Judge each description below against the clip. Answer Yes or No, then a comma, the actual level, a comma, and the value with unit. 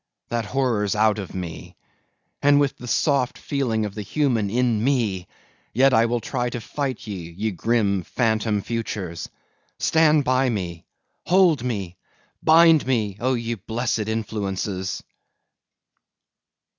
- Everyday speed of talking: No, slow, 130 wpm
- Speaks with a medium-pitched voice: No, low, 115 Hz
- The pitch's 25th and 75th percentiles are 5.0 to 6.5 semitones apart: No, average, 4.1 semitones